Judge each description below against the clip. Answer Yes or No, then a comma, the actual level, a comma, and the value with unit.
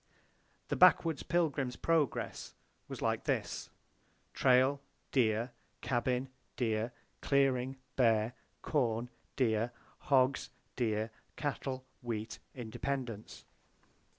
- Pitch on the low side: Yes, low, 125 Hz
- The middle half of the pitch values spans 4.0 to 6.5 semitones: No, average, 3.1 semitones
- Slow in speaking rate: Yes, slow, 85 wpm